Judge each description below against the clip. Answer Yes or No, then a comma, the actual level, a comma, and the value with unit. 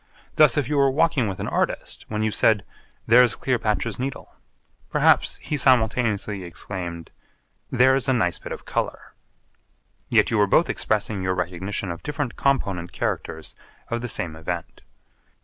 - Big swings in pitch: Yes, wide, 5.9 semitones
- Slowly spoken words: No, average, 150 wpm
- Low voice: Yes, low, 110 Hz